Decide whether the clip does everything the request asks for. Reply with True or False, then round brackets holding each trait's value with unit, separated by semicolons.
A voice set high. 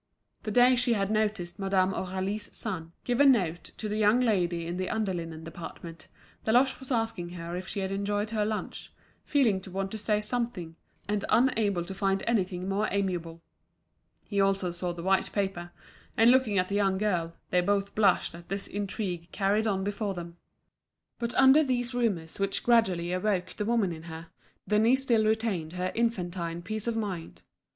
True (195 Hz)